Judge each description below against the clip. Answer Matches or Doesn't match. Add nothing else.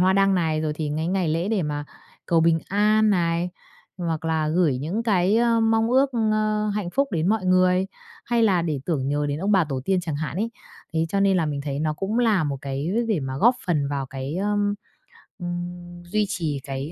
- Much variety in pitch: Doesn't match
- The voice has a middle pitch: Matches